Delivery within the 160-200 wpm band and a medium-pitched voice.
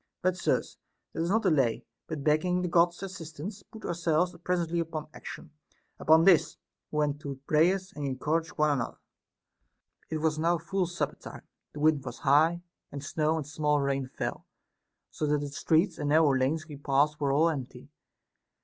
Yes: average, 185 wpm; medium, 155 Hz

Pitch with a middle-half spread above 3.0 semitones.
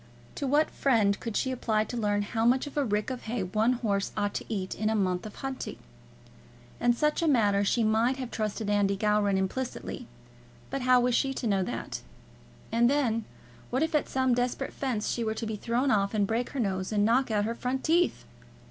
Yes: average, 3.7 semitones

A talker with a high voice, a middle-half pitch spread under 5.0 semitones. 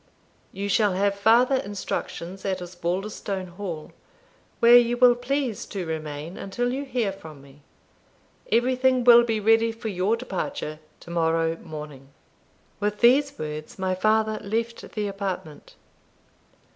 No: high, 200 Hz; average, 5.3 semitones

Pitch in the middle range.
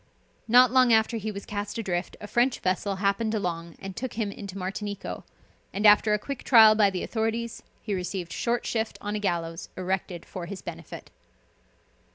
No: high, 205 Hz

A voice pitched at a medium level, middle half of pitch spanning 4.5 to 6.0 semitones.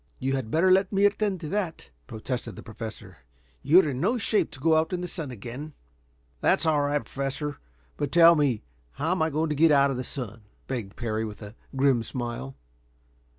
Yes: medium, 145 Hz; average, 4.8 semitones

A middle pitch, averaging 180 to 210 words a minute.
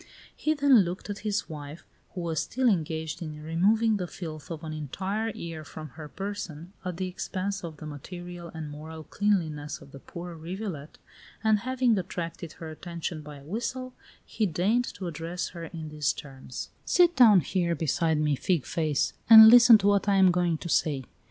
Yes: medium, 170 Hz; average, 185 wpm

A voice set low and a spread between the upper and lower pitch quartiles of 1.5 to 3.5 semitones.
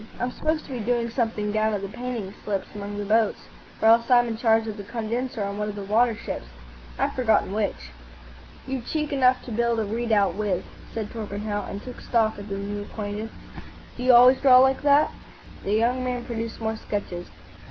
No: high, 225 Hz; average, 3.1 semitones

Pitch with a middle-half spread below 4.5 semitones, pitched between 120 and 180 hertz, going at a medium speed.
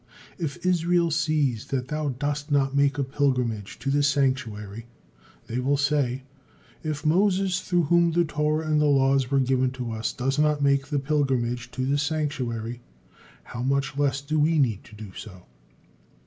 Yes: average, 3.1 semitones; medium, 140 Hz; average, 170 wpm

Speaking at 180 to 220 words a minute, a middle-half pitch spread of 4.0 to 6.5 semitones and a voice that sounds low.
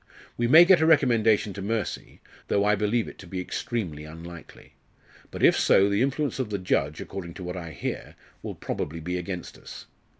Yes: average, 195 wpm; average, 5.2 semitones; low, 100 Hz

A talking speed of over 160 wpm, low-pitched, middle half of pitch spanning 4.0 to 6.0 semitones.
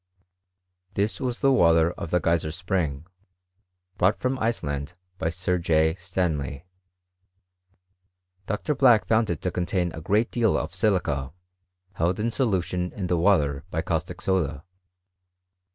No: average, 140 wpm; very low, 90 Hz; average, 4.5 semitones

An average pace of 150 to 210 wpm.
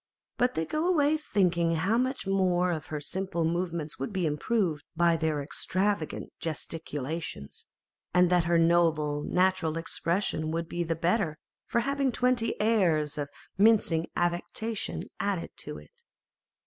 No: average, 140 wpm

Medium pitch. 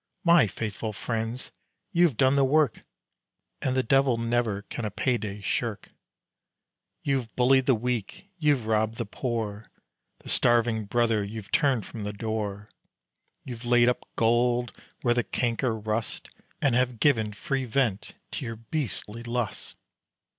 No: low, 120 Hz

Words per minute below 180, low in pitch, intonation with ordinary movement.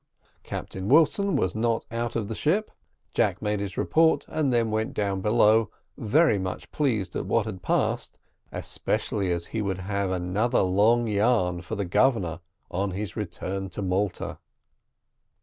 Yes: average, 155 wpm; low, 105 Hz; average, 3.7 semitones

